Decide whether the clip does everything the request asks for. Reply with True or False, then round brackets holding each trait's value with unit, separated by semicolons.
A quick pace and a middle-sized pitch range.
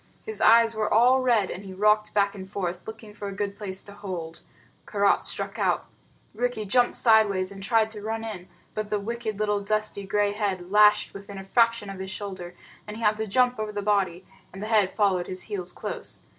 False (210 wpm; 2.0 semitones)